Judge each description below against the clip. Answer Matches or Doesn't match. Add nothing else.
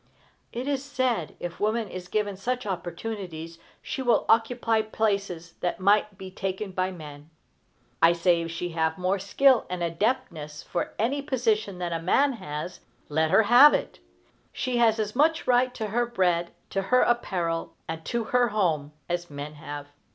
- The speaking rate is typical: Matches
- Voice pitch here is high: Matches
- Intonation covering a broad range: Matches